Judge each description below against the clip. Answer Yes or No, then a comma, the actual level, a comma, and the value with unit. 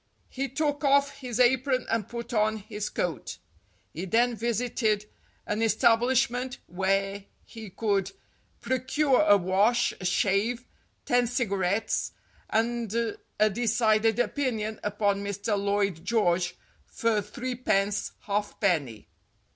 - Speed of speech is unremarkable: No, slow, 115 wpm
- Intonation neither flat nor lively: Yes, average, 3.5 semitones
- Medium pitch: No, high, 220 Hz